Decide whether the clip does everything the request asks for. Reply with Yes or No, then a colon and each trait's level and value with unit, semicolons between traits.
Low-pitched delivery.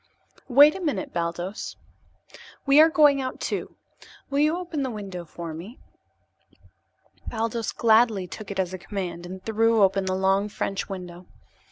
No: high, 205 Hz